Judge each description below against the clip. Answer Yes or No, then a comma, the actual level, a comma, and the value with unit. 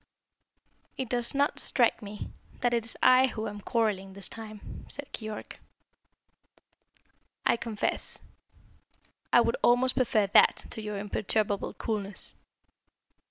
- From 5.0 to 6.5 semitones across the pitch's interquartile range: No, average, 2.9 semitones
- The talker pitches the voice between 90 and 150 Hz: No, high, 220 Hz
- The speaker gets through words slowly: Yes, slow, 120 wpm